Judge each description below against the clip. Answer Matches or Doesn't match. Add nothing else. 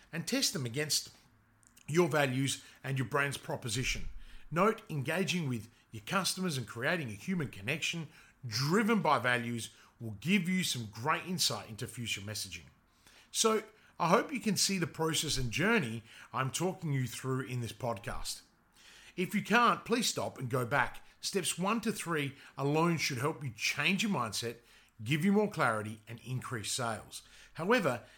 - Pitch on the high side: Doesn't match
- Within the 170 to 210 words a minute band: Doesn't match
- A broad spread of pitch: Matches